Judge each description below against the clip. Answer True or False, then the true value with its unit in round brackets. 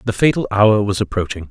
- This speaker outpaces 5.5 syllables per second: True (5.8 syllables/s)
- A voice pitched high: False (105 Hz)